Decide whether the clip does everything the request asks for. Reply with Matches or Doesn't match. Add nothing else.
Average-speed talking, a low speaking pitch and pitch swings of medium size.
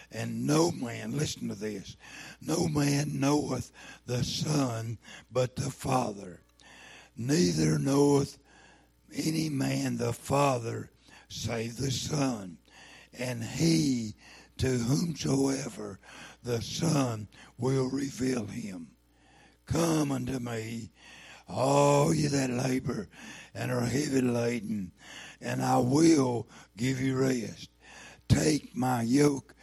Doesn't match